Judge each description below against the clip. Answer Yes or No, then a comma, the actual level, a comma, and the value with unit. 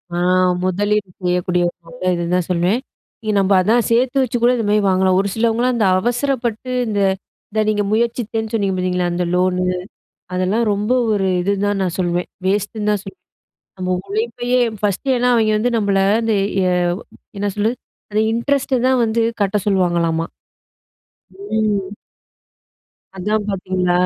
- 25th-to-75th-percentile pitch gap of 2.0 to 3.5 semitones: No, average, 3.9 semitones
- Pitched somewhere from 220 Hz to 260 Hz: No, high, 205 Hz